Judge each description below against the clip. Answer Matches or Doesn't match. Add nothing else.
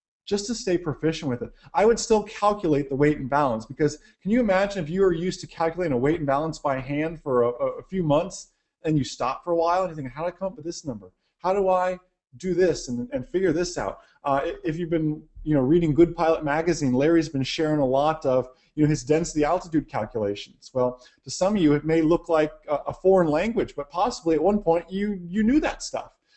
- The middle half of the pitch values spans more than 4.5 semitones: Doesn't match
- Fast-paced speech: Matches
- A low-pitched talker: Doesn't match